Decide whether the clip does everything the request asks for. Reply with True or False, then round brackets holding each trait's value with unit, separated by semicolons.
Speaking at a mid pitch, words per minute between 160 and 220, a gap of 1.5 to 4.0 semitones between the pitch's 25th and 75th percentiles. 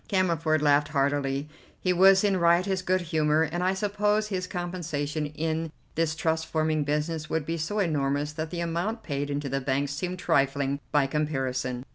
True (155 Hz; 170 wpm; 3.6 semitones)